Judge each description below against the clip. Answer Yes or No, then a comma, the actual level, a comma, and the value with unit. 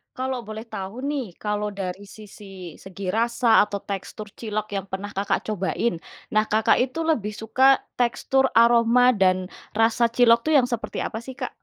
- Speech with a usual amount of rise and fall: Yes, average, 3.2 semitones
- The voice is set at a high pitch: Yes, high, 220 Hz